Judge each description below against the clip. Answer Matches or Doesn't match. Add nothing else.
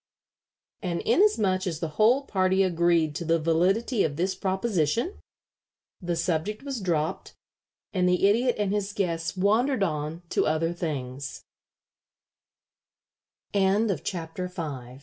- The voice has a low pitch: Doesn't match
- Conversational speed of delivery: Doesn't match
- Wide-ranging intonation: Doesn't match